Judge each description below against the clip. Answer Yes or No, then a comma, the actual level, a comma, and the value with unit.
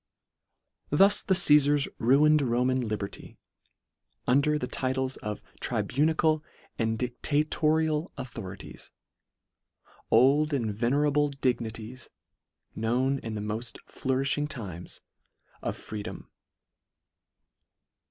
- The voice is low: Yes, low, 130 Hz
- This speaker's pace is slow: Yes, slow, 90 wpm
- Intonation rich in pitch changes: No, average, 4.5 semitones